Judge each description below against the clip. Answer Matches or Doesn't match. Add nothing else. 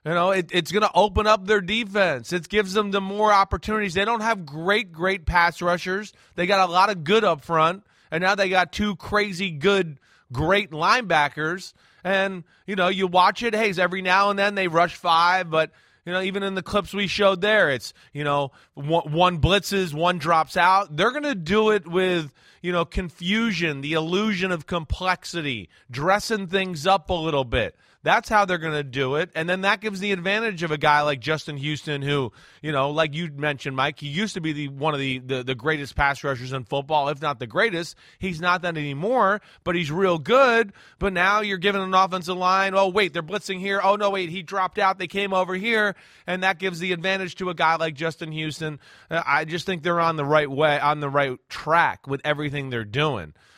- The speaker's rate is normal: Doesn't match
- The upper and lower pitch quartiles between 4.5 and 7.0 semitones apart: Doesn't match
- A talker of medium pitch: Matches